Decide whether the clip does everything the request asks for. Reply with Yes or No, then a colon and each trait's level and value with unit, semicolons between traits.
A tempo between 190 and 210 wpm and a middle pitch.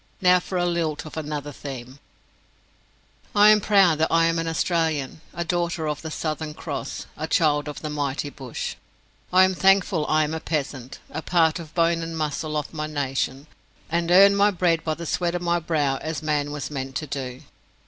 Yes: average, 200 wpm; medium, 160 Hz